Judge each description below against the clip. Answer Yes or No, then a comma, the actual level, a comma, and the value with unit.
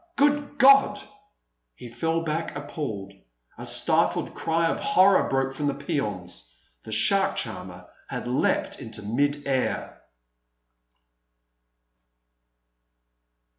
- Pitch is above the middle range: No, medium, 145 Hz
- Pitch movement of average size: No, wide, 6.9 semitones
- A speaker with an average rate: No, slow, 100 wpm